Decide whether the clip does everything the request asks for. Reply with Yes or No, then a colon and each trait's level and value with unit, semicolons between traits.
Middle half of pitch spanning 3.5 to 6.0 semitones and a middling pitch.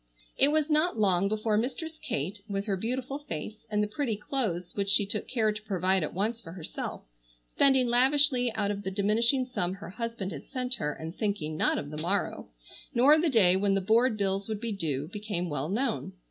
No: average, 4.5 semitones; high, 210 Hz